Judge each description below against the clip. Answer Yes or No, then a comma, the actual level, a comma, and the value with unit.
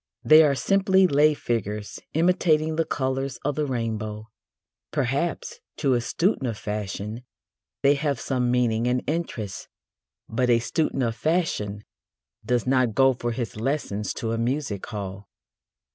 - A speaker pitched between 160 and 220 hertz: No, low, 125 Hz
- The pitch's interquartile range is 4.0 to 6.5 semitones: Yes, average, 5.0 semitones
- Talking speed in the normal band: Yes, average, 145 wpm